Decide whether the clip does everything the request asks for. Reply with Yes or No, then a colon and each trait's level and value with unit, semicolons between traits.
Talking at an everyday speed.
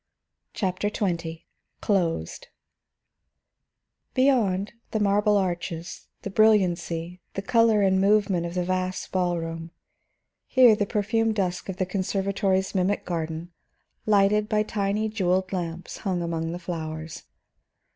No: slow, 120 wpm